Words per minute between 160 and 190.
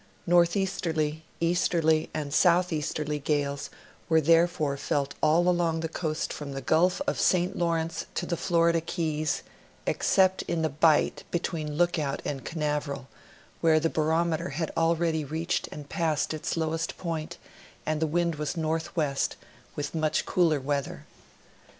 No: average, 140 wpm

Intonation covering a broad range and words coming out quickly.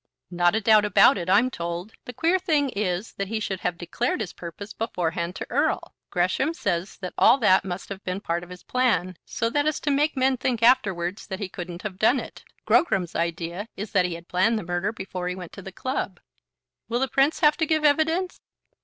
Yes: wide, 6.2 semitones; fast, 215 wpm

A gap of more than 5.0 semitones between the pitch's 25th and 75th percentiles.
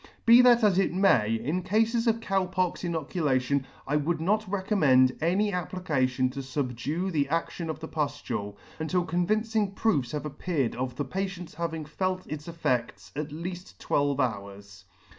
Yes: wide, 5.6 semitones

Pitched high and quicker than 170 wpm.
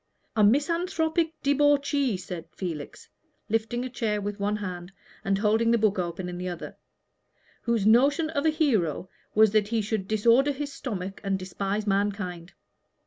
No: high, 215 Hz; average, 155 wpm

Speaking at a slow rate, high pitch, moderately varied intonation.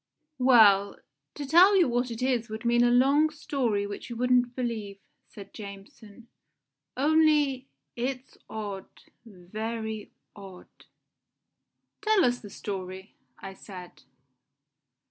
Yes: slow, 115 wpm; high, 235 Hz; average, 4.4 semitones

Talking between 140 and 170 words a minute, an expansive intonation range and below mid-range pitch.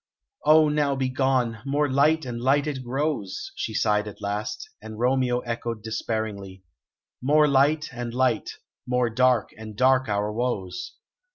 No: average, 150 wpm; average, 3.9 semitones; low, 125 Hz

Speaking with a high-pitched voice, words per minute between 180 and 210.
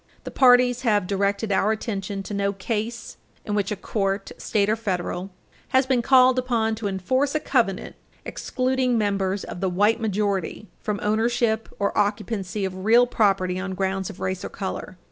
No: high, 210 Hz; average, 170 wpm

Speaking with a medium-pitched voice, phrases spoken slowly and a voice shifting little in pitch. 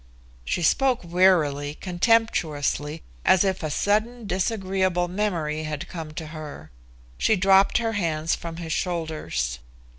No: medium, 175 Hz; slow, 125 wpm; average, 4.0 semitones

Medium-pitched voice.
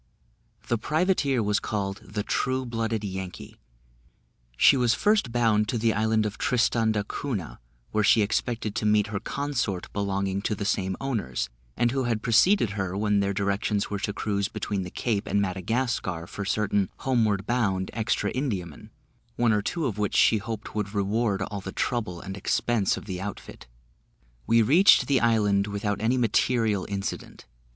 No: low, 105 Hz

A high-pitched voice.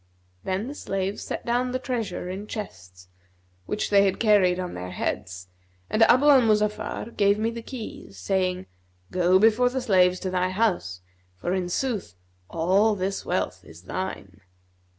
Yes: high, 195 Hz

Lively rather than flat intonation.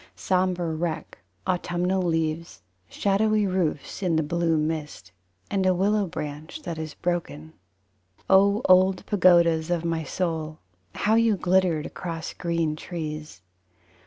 No: average, 2.9 semitones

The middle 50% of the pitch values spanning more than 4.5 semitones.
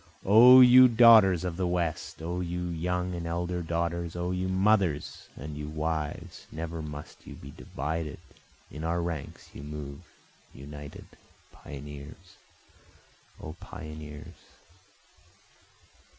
No: average, 3.0 semitones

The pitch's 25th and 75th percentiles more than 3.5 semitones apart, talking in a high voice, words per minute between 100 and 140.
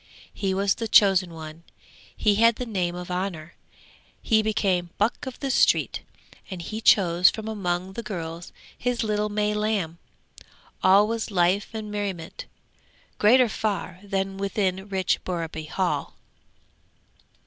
No: average, 3.2 semitones; high, 195 Hz; slow, 135 wpm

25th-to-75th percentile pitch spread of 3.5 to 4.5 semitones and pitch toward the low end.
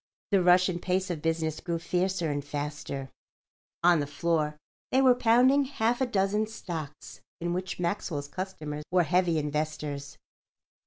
No: average, 4.1 semitones; medium, 175 Hz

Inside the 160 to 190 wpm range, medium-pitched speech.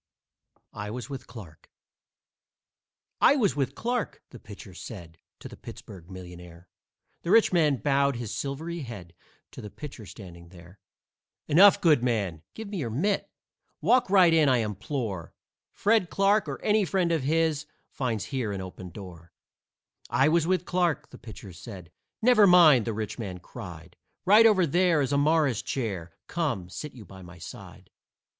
No: average, 165 wpm; low, 130 Hz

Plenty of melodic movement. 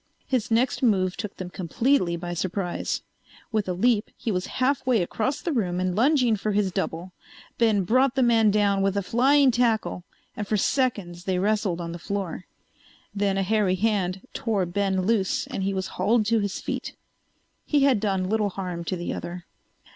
No: average, 3.8 semitones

